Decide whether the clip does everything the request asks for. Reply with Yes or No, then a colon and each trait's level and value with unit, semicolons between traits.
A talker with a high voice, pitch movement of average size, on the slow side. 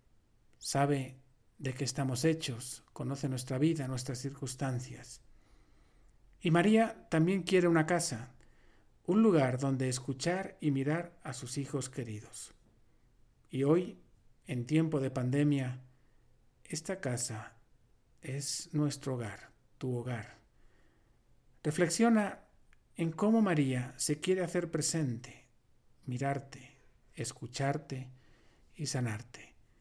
No: low, 135 Hz; average, 4.1 semitones; slow, 105 wpm